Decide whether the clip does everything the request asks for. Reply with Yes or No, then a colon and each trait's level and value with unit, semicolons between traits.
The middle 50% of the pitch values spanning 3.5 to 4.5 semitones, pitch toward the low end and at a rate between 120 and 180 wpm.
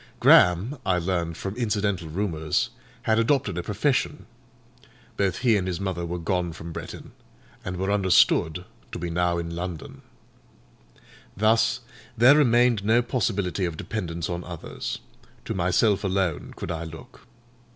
Yes: average, 4.2 semitones; very low, 95 Hz; average, 140 wpm